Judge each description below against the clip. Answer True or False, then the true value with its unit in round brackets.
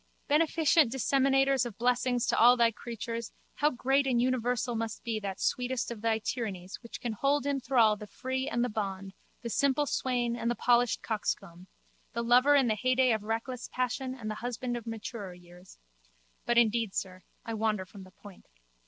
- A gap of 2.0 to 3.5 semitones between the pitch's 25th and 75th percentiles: True (2.9 semitones)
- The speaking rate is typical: True (185 wpm)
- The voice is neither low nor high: False (235 Hz)